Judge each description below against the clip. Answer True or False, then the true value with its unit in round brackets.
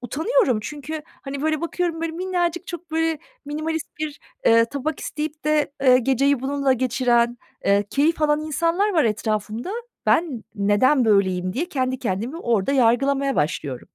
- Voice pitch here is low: False (280 Hz)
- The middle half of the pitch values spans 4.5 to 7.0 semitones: True (5.1 semitones)